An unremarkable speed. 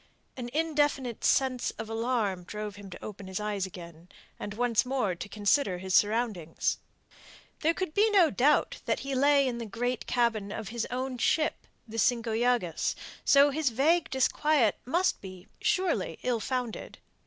Yes: average, 165 wpm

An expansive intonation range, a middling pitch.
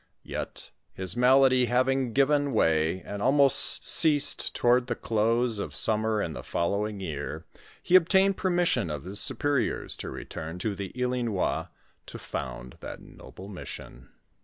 No: wide, 6.0 semitones; low, 115 Hz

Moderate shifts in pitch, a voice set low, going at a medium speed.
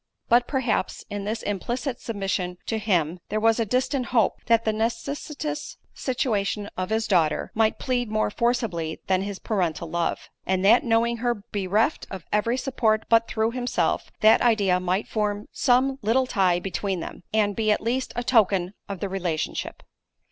No: average, 3.6 semitones; high, 215 Hz; average, 170 wpm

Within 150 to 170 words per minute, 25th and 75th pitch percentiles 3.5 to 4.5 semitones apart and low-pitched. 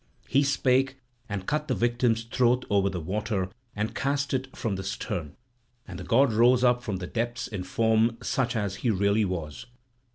No: average, 185 wpm; average, 4.2 semitones; low, 115 Hz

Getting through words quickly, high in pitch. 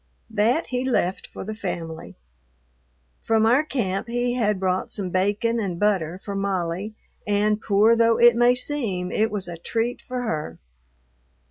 No: average, 155 wpm; high, 210 Hz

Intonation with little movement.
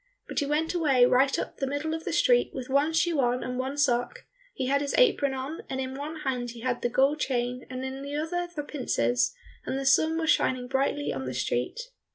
No: average, 3.3 semitones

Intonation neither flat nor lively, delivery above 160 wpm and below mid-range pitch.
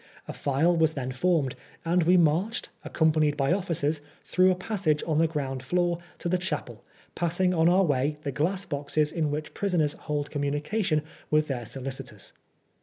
No: average, 3.4 semitones; average, 170 wpm; medium, 155 Hz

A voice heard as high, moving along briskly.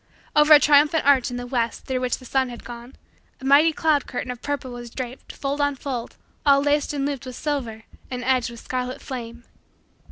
Yes: very high, 260 Hz; fast, 210 wpm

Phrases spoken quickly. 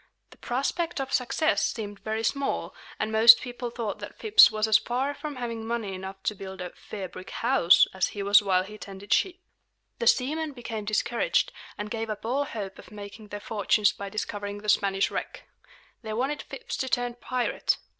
No: average, 190 wpm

